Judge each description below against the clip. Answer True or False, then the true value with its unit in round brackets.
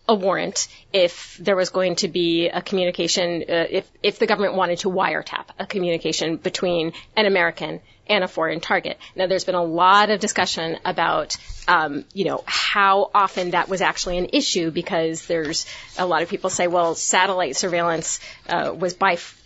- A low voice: False (185 Hz)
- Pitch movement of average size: False (2.3 semitones)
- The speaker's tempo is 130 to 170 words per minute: False (180 wpm)